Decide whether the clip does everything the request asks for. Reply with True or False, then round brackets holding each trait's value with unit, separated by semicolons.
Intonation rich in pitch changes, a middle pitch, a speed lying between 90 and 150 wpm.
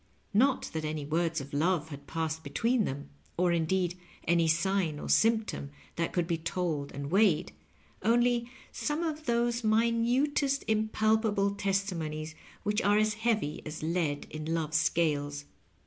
True (5.9 semitones; 180 Hz; 145 wpm)